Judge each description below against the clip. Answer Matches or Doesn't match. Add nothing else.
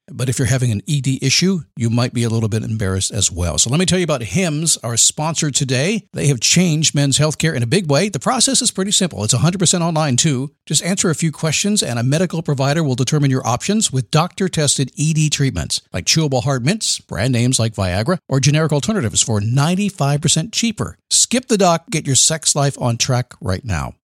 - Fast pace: Matches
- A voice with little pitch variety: Doesn't match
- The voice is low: Doesn't match